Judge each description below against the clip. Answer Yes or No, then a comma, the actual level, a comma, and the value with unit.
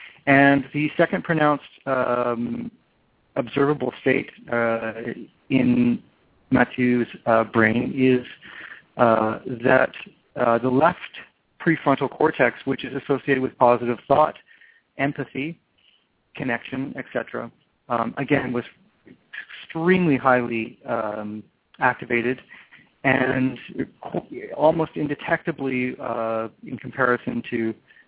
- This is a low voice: Yes, low, 130 Hz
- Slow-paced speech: Yes, slow, 90 wpm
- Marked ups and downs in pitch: No, average, 2.9 semitones